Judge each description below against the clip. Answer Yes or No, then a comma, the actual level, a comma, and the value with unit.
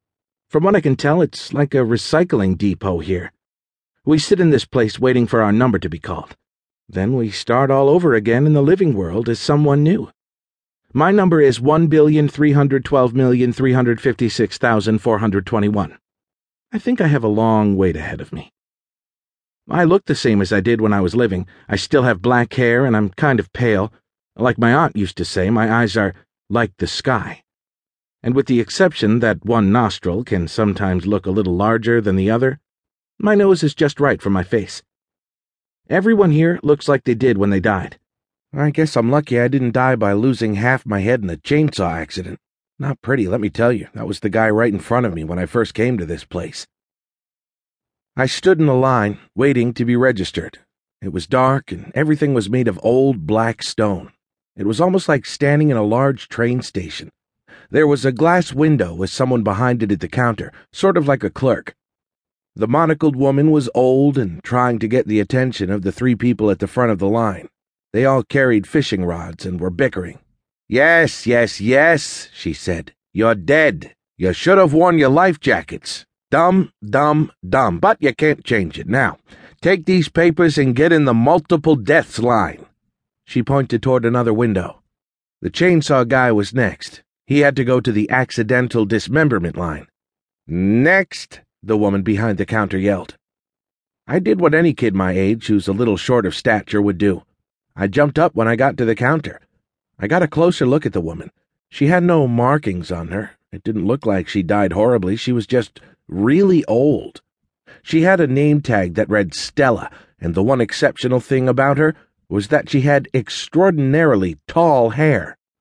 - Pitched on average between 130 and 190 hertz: No, low, 120 Hz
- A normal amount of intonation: No, wide, 5.9 semitones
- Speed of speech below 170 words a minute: No, average, 185 wpm